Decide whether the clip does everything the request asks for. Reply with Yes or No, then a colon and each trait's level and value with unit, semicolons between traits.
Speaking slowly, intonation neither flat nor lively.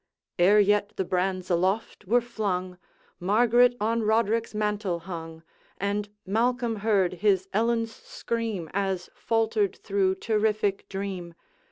Yes: slow, 120 wpm; average, 3.1 semitones